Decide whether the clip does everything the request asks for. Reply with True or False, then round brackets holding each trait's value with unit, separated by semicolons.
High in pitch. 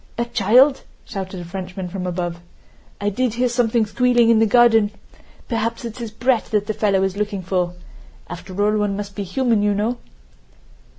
True (210 Hz)